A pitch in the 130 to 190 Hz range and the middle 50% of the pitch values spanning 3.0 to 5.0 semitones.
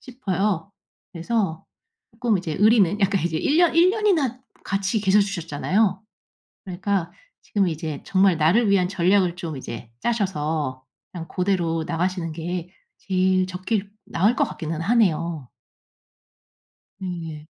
Yes: medium, 185 Hz; average, 3.7 semitones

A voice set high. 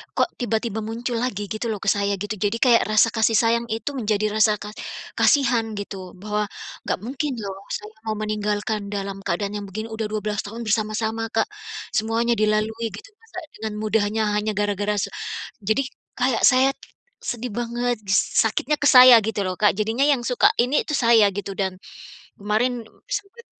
Yes: high, 220 Hz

